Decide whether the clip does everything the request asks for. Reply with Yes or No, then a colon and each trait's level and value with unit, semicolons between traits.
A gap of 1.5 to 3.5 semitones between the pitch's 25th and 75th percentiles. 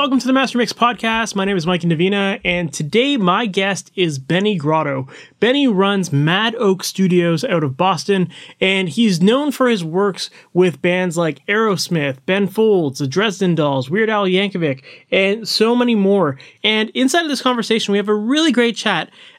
No: average, 4.3 semitones